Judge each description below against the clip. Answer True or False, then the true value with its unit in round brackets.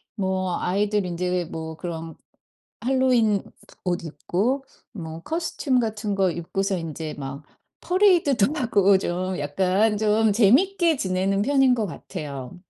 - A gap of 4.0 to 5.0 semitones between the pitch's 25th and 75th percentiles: False (5.4 semitones)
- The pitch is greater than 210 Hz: False (195 Hz)